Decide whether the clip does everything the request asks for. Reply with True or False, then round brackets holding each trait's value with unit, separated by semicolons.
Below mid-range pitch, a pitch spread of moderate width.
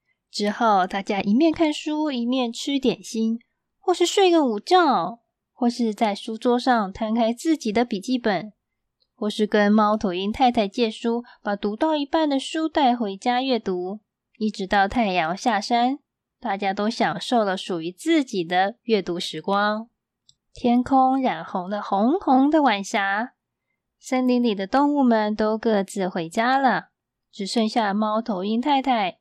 False (230 Hz; 4.0 semitones)